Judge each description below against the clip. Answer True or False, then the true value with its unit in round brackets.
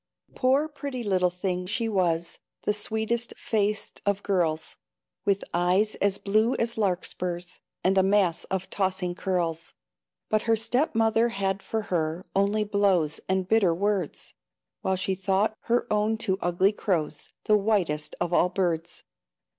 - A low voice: False (195 Hz)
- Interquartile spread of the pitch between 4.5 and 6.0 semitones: False (3.2 semitones)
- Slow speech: False (145 wpm)